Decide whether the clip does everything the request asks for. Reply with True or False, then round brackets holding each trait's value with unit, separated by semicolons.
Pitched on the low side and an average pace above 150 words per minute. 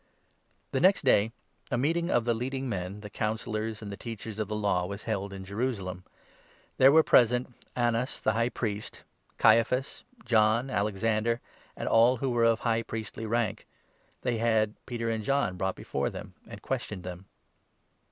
True (115 Hz; 180 wpm)